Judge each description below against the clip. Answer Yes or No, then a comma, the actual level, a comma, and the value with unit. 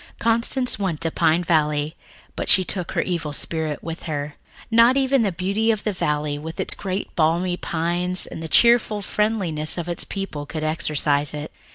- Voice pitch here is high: No, medium, 170 Hz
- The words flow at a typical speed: Yes, average, 180 wpm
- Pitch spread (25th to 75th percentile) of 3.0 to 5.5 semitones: Yes, average, 4.5 semitones